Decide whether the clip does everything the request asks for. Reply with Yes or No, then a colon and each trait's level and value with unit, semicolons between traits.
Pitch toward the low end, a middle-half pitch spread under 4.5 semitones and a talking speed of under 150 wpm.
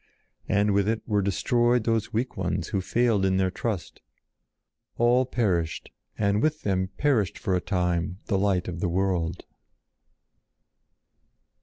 Yes: low, 100 Hz; average, 3.8 semitones; average, 140 wpm